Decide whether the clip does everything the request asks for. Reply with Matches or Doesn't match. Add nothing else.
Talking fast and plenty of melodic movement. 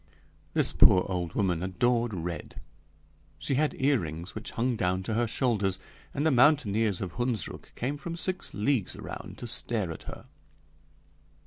Doesn't match